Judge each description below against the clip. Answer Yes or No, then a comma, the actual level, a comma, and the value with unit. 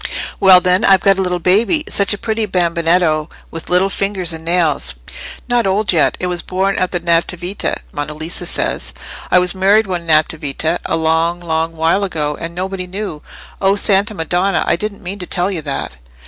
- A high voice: No, medium, 180 Hz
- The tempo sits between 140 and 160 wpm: No, average, 190 wpm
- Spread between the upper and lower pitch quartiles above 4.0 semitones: No, average, 2.9 semitones